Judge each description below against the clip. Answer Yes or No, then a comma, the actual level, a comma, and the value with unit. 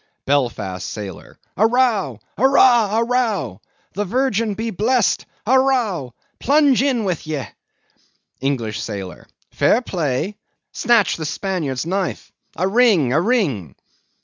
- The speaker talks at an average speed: No, slow, 120 wpm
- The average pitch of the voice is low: No, high, 195 Hz